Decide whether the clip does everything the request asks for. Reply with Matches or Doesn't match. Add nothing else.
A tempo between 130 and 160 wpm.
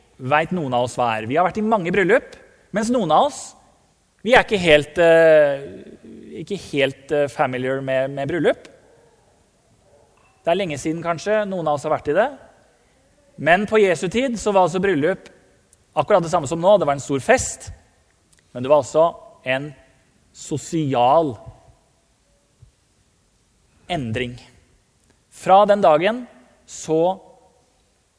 Matches